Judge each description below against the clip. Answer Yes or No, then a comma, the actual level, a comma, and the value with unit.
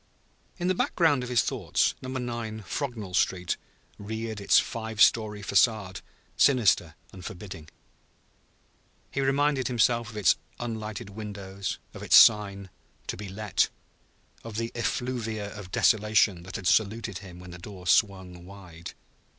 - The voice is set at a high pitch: No, low, 105 Hz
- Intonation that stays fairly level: No, average, 3.4 semitones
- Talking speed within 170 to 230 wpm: No, average, 140 wpm